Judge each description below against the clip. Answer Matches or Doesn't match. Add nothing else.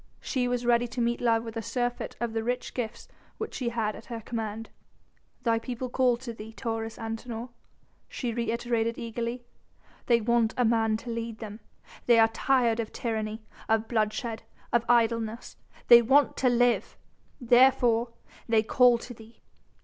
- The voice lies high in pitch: Matches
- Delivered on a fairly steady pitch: Matches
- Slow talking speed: Doesn't match